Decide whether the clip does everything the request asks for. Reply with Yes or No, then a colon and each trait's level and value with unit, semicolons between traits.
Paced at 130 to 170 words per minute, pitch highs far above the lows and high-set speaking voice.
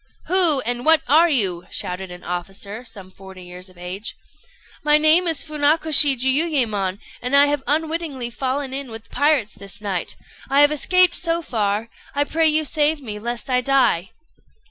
Yes: average, 165 wpm; wide, 7.0 semitones; very high, 265 Hz